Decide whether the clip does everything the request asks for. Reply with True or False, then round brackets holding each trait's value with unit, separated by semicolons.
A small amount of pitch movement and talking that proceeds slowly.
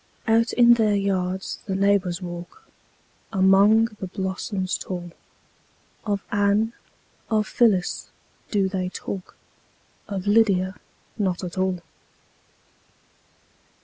True (2.2 semitones; 100 wpm)